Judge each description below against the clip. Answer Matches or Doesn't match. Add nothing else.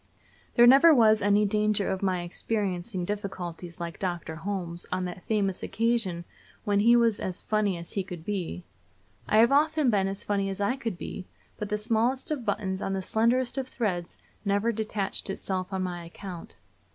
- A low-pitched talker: Doesn't match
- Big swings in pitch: Doesn't match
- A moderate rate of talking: Matches